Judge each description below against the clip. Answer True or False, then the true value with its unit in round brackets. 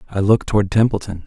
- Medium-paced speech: True (190 wpm)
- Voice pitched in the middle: False (100 Hz)